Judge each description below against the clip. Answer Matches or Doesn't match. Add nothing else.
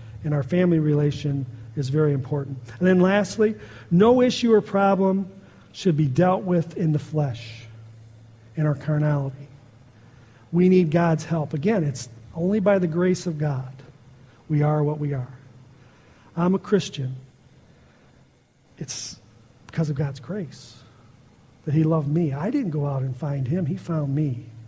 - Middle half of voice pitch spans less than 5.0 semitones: Doesn't match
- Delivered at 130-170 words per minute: Matches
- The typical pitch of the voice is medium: Matches